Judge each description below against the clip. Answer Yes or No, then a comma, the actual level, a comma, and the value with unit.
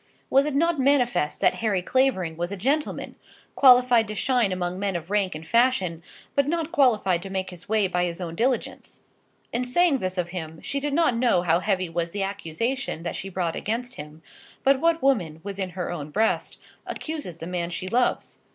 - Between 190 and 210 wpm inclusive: Yes, average, 195 wpm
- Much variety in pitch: Yes, wide, 6.6 semitones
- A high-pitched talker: Yes, high, 200 Hz